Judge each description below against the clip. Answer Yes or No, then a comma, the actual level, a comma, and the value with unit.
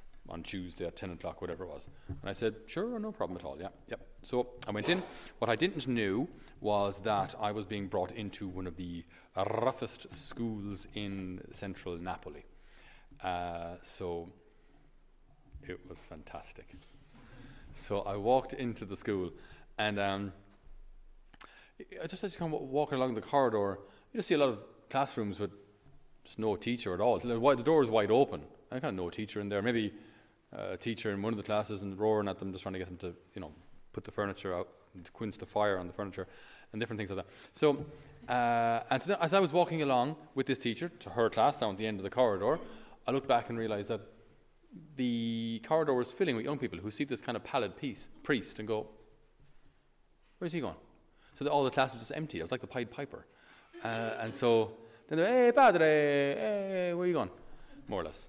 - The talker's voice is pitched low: Yes, low, 110 Hz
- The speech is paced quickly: Yes, fast, 210 wpm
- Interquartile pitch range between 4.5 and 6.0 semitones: Yes, average, 5.1 semitones